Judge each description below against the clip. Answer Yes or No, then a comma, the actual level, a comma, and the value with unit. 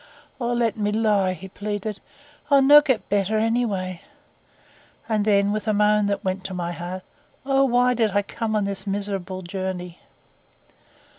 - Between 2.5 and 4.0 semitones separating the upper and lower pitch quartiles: Yes, average, 2.9 semitones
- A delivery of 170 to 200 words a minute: No, average, 160 wpm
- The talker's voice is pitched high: Yes, high, 205 Hz